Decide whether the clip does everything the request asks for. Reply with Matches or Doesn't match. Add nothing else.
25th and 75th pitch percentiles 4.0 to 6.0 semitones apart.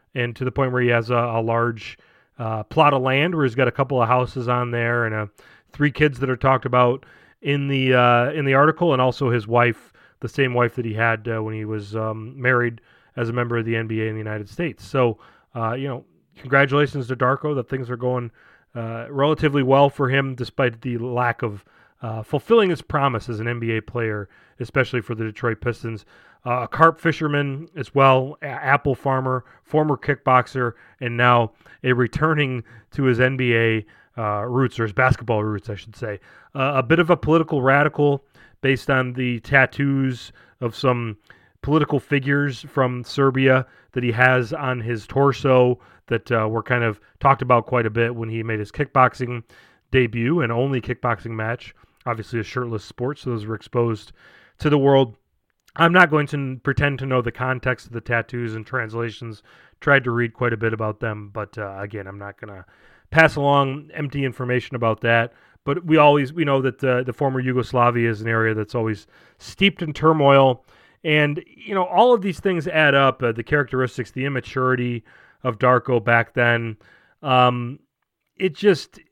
Doesn't match